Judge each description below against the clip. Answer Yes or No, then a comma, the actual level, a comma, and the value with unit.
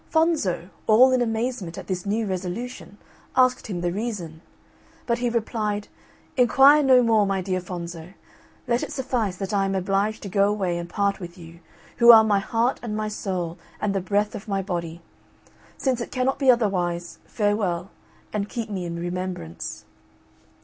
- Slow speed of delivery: No, average, 170 wpm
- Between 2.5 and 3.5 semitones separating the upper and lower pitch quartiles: No, average, 4.5 semitones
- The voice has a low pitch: No, high, 205 Hz